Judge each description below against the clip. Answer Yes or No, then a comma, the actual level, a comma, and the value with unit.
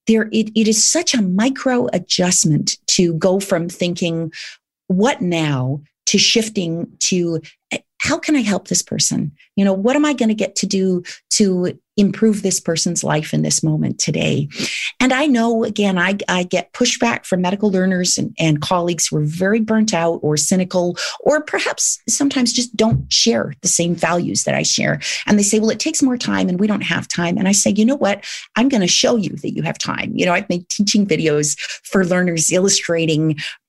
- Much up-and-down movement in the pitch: No, average, 4.2 semitones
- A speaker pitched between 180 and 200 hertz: Yes, high, 190 Hz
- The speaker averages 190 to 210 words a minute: Yes, average, 200 wpm